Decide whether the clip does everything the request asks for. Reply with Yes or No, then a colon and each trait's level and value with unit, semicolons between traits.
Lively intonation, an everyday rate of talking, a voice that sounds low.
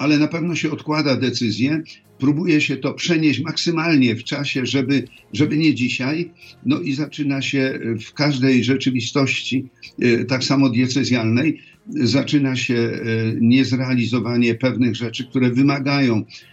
No: average, 2.8 semitones; average, 125 wpm; low, 130 Hz